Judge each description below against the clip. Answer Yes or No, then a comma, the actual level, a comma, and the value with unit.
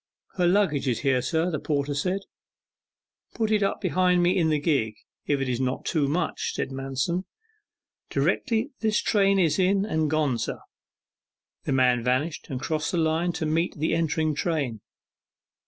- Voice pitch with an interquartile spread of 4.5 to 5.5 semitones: Yes, average, 4.8 semitones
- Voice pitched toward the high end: No, medium, 155 Hz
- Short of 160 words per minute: No, average, 170 wpm